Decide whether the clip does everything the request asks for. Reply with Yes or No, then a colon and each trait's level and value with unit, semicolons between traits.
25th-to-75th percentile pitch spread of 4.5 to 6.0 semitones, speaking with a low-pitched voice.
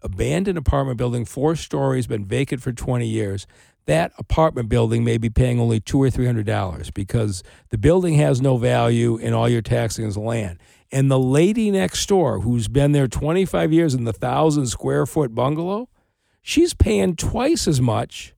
Yes: average, 4.9 semitones; low, 125 Hz